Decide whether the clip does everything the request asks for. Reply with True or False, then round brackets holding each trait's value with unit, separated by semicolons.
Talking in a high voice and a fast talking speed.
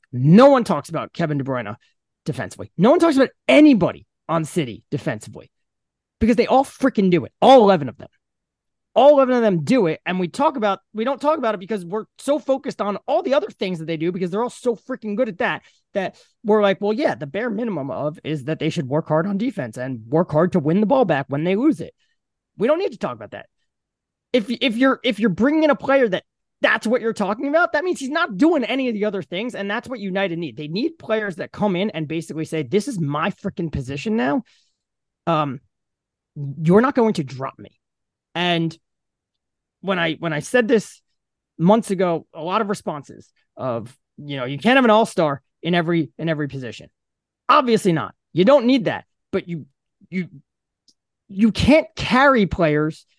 True (200 Hz; 215 wpm)